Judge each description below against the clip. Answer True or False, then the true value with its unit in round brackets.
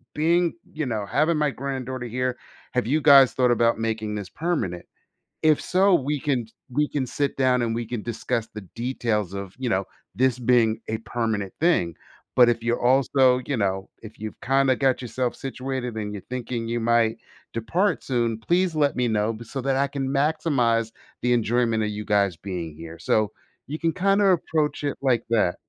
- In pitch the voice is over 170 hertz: False (125 Hz)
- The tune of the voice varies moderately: True (3.7 semitones)